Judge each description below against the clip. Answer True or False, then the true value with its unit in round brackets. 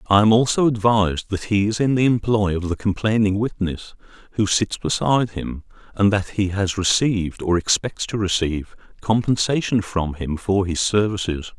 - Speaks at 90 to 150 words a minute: False (170 wpm)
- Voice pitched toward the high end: False (100 Hz)